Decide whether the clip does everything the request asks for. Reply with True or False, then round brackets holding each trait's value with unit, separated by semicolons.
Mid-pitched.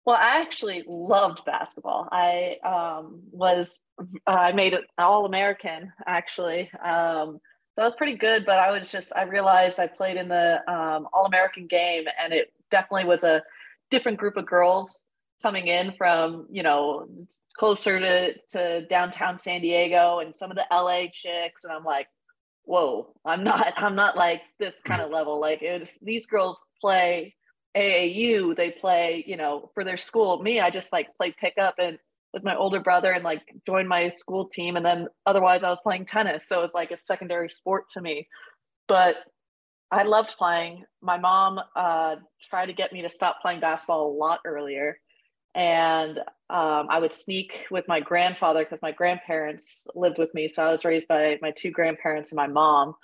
True (180 Hz)